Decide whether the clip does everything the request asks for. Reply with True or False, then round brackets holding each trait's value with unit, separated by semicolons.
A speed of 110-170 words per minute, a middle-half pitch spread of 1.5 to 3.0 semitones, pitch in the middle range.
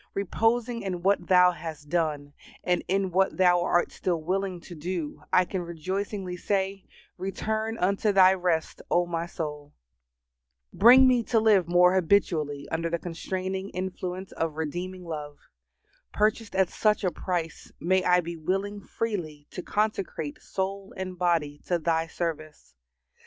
True (145 wpm; 2.7 semitones; 180 Hz)